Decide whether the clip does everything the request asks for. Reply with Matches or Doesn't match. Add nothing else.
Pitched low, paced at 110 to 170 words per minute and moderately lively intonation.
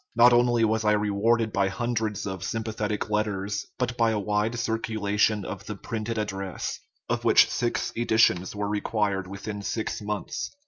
Doesn't match